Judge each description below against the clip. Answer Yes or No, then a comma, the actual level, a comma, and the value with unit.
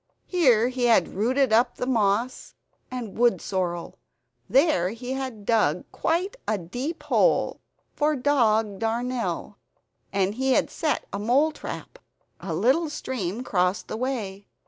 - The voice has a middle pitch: No, high, 235 Hz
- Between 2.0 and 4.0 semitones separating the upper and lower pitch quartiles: No, average, 4.7 semitones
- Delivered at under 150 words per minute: Yes, slow, 135 wpm